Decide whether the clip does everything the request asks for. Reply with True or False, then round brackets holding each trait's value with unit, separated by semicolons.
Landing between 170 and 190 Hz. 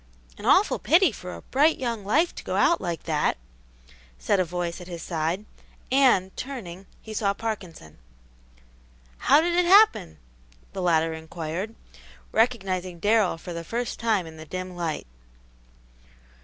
True (185 Hz)